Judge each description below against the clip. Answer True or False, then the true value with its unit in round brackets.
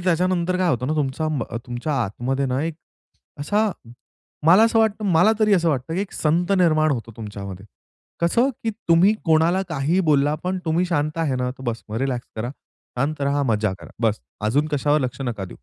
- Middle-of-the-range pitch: True (155 Hz)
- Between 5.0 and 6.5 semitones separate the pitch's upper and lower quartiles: True (5.6 semitones)